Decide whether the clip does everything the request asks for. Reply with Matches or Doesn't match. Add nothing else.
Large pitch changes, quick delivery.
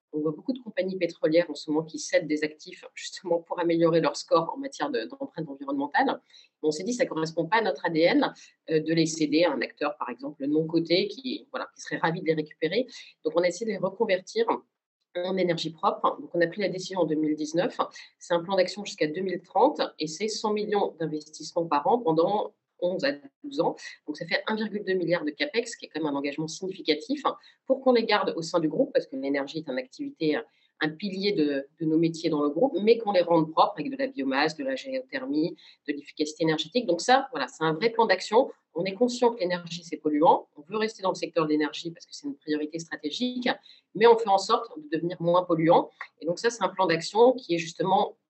Matches